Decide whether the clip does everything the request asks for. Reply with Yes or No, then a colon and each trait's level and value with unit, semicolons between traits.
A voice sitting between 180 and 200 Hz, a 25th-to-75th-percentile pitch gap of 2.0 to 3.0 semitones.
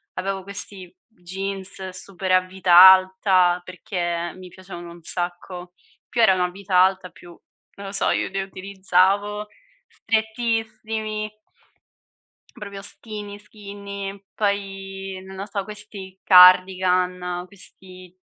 No: high, 190 Hz; narrow, 1.6 semitones